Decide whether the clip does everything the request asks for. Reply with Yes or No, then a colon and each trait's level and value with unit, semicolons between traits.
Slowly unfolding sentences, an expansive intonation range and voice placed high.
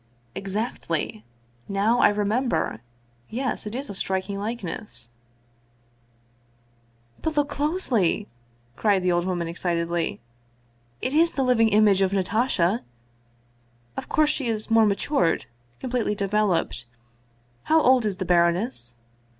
Yes: slow, 125 wpm; wide, 5.8 semitones; high, 200 Hz